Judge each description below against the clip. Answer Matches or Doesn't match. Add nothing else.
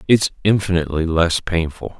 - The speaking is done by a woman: Doesn't match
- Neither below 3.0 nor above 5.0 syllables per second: Doesn't match